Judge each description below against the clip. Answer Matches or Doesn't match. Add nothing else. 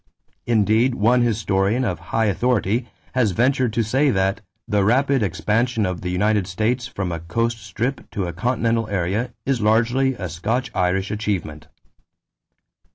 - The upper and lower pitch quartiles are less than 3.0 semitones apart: Doesn't match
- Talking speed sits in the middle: Matches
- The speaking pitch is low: Matches